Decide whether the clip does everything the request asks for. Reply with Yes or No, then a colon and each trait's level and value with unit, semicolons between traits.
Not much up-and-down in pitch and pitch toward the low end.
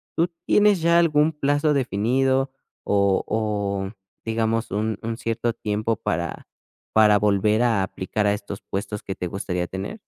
No: average, 4.8 semitones; low, 110 Hz